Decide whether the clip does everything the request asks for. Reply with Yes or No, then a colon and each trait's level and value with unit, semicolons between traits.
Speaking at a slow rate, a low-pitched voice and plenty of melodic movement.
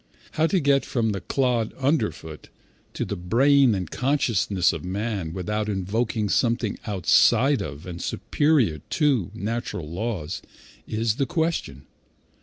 Yes: slow, 130 wpm; low, 110 Hz; wide, 6.5 semitones